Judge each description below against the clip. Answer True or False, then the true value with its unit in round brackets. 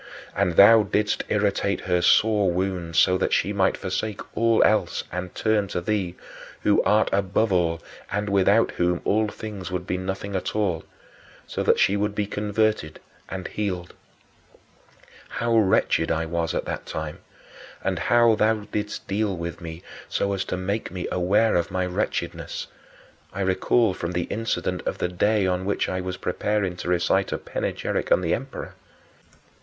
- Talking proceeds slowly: False (170 wpm)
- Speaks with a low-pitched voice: True (95 Hz)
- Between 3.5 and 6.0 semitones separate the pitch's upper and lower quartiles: False (2.8 semitones)